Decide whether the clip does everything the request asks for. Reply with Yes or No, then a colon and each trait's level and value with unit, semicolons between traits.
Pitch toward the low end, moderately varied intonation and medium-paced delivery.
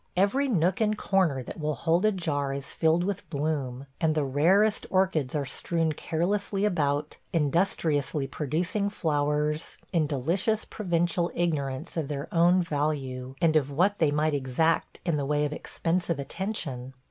No: medium, 160 Hz; average, 3.9 semitones; average, 155 wpm